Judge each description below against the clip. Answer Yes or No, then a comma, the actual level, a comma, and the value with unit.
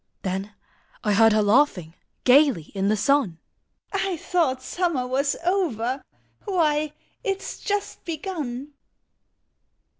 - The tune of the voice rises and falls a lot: Yes, wide, 7.6 semitones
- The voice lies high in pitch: Yes, very high, 275 Hz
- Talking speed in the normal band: No, slow, 120 wpm